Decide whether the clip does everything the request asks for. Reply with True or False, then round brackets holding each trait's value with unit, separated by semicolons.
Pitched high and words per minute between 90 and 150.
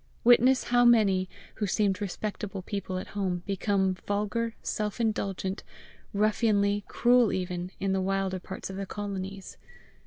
True (200 Hz; 135 wpm)